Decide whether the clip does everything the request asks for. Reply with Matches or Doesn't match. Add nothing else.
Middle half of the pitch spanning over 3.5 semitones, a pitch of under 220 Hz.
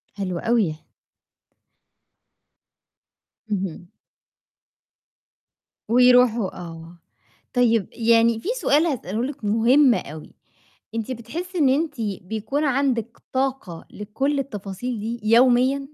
Doesn't match